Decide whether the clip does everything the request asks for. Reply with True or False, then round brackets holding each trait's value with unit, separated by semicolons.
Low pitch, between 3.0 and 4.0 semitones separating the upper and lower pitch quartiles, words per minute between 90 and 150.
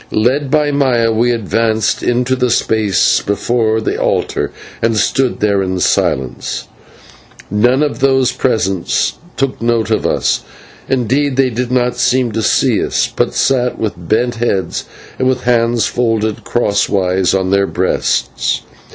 True (115 Hz; 3.3 semitones; 145 wpm)